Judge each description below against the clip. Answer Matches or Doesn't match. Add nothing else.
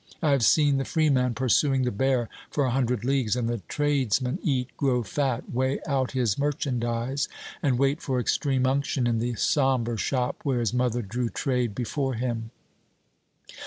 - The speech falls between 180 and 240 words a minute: Doesn't match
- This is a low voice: Matches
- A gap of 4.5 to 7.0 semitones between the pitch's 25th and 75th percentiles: Doesn't match